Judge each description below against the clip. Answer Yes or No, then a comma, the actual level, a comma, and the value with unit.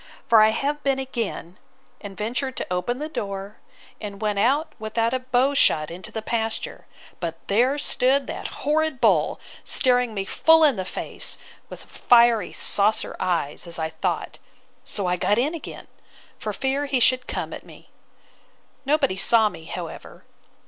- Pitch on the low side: No, high, 230 Hz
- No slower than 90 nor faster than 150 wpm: No, average, 165 wpm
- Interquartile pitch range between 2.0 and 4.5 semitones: No, average, 5.2 semitones